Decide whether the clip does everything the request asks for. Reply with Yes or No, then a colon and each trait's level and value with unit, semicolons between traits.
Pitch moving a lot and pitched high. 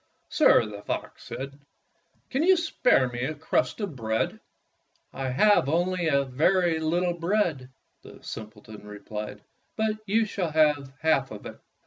No: wide, 6.3 semitones; medium, 155 Hz